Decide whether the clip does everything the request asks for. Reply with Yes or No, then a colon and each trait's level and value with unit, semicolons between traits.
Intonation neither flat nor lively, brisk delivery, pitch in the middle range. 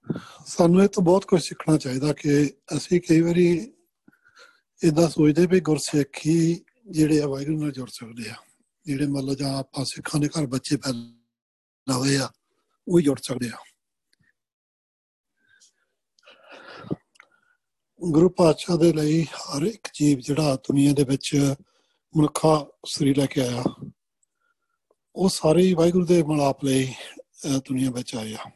No: average, 4.3 semitones; average, 125 wpm; medium, 155 Hz